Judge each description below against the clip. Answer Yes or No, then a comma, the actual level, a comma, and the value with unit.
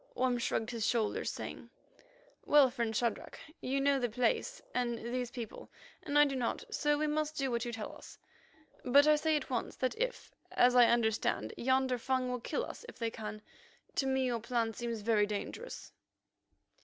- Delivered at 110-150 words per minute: No, average, 185 wpm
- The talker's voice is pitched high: Yes, very high, 250 Hz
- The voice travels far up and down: No, average, 2.9 semitones